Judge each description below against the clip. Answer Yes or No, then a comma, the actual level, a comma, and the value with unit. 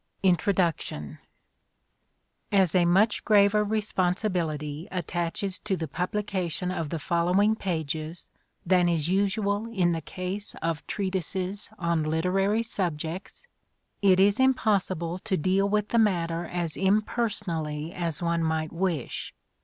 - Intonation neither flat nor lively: Yes, average, 3.3 semitones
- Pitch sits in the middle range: Yes, medium, 180 Hz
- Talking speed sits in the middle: No, slow, 120 wpm